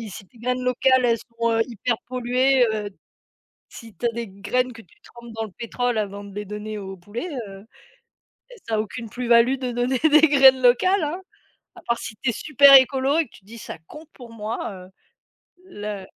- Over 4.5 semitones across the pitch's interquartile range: No, average, 3.3 semitones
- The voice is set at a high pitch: Yes, high, 235 Hz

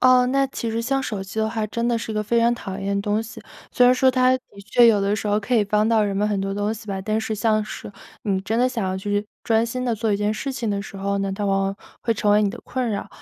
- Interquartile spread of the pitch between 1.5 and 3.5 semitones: Yes, narrow, 2.6 semitones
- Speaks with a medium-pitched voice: No, high, 215 Hz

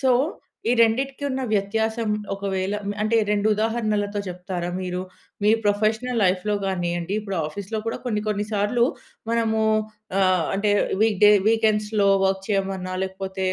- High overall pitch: Yes, high, 205 Hz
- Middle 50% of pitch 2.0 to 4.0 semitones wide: Yes, narrow, 2.6 semitones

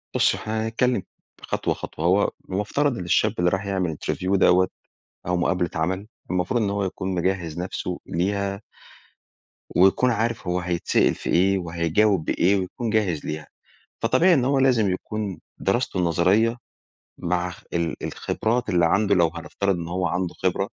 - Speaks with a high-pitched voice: No, very low, 95 Hz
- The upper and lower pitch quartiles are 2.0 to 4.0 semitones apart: Yes, average, 3.4 semitones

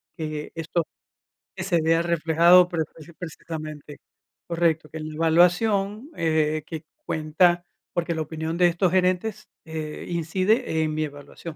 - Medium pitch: Yes, medium, 165 Hz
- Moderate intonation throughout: No, narrow, 2.1 semitones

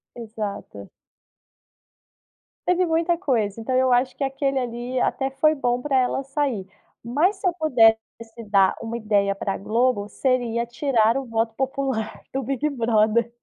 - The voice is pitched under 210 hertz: No, very high, 250 Hz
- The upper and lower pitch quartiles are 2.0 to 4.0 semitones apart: Yes, average, 3.4 semitones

